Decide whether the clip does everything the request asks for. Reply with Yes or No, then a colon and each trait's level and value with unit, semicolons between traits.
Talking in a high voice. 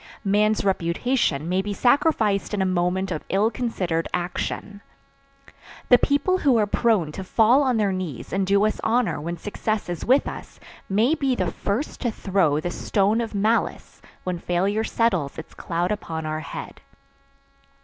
Yes: high, 200 Hz